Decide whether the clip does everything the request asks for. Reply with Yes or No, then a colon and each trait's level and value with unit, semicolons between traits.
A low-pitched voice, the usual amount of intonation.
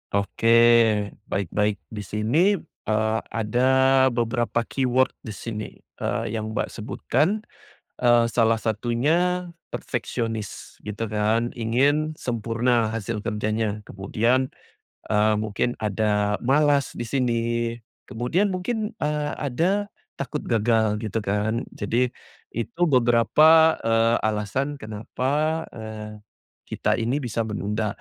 Yes: low, 115 Hz; average, 3.6 semitones